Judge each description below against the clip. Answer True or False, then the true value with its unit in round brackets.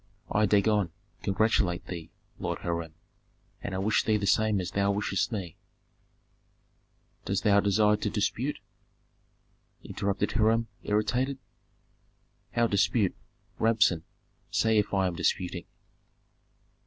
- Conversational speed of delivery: False (115 wpm)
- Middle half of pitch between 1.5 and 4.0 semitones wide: True (2.4 semitones)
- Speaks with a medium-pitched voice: False (100 Hz)